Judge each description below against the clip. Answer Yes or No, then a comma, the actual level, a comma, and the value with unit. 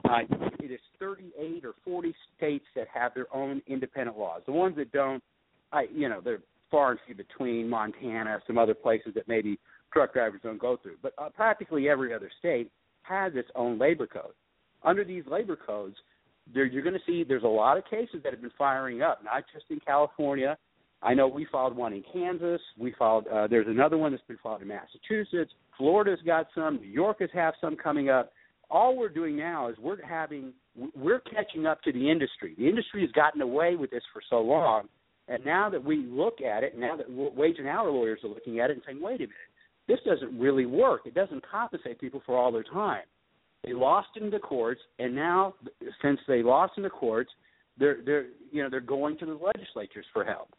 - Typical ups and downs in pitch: No, wide, 7.0 semitones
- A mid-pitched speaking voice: Yes, medium, 145 Hz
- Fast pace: Yes, fast, 210 wpm